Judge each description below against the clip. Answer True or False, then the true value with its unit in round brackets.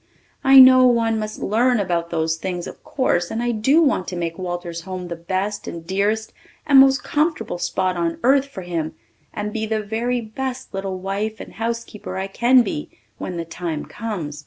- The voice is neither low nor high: False (205 Hz)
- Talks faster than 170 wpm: True (190 wpm)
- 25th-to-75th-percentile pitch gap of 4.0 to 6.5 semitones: True (5.3 semitones)